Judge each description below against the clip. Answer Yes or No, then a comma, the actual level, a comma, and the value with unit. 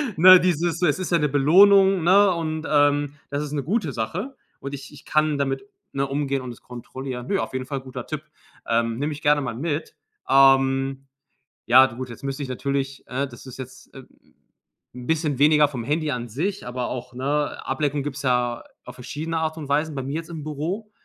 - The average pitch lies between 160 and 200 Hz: No, medium, 140 Hz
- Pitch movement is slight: No, average, 3.1 semitones